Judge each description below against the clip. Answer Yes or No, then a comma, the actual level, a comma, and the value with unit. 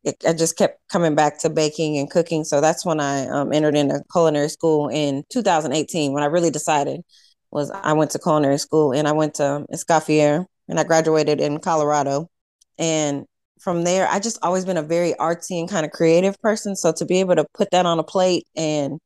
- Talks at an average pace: No, fast, 210 wpm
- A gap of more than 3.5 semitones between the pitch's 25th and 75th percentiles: No, narrow, 2.5 semitones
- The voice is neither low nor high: Yes, medium, 160 Hz